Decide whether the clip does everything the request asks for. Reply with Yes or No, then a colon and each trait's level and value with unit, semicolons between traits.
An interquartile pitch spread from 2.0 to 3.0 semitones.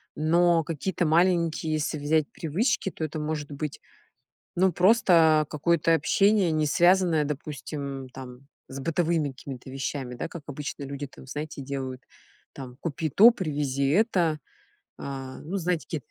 No: average, 3.5 semitones